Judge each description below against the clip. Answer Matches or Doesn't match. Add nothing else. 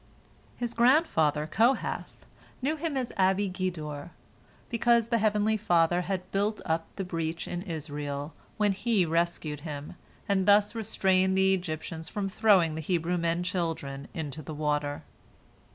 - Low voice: Doesn't match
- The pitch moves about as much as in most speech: Matches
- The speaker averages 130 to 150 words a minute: Matches